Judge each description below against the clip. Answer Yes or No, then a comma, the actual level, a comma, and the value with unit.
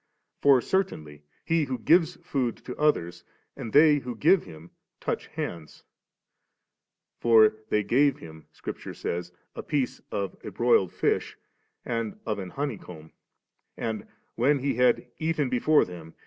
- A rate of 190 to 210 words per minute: No, average, 155 wpm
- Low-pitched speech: Yes, low, 120 Hz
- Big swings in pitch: Yes, wide, 7.9 semitones